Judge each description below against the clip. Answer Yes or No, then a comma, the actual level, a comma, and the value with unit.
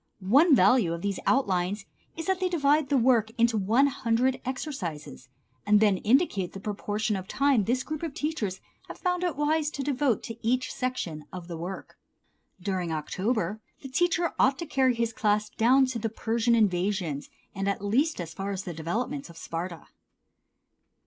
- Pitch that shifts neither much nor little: No, wide, 6.0 semitones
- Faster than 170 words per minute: Yes, average, 180 wpm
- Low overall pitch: No, high, 225 Hz